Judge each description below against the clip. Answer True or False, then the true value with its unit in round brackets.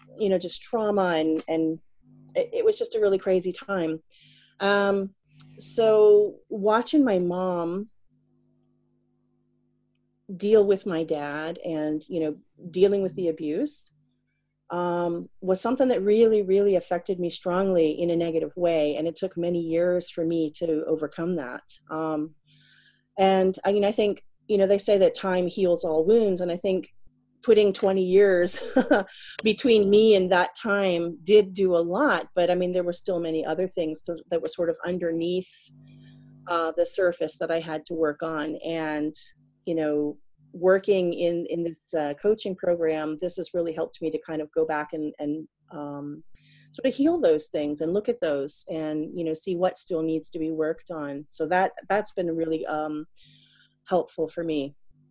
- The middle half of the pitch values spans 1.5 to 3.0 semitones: False (3.5 semitones)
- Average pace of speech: True (170 wpm)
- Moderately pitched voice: True (170 Hz)